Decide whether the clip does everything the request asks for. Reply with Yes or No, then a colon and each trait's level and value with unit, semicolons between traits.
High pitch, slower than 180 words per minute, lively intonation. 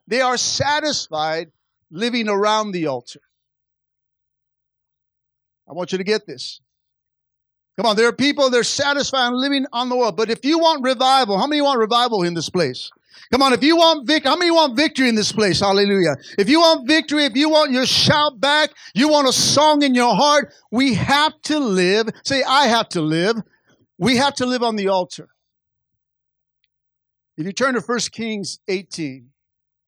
No: high, 240 Hz; average, 185 wpm; wide, 6.5 semitones